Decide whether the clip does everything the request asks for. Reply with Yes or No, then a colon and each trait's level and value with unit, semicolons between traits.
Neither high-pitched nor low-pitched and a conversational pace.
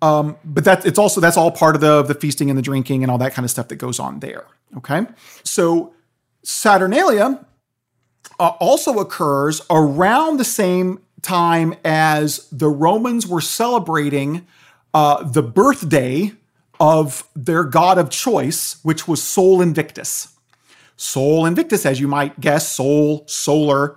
Yes: medium, 155 Hz; average, 150 wpm